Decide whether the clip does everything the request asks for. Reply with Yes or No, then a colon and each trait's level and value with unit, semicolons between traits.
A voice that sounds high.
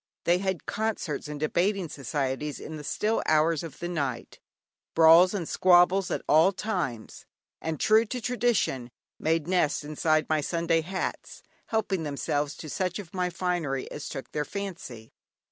No: medium, 165 Hz